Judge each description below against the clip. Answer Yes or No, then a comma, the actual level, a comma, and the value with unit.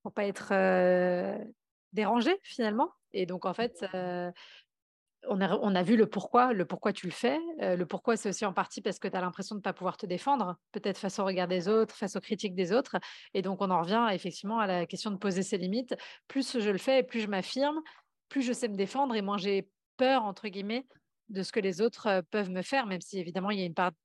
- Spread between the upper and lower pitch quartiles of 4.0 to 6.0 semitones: No, average, 3.6 semitones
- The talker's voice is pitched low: No, high, 205 Hz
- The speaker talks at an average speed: No, fast, 245 wpm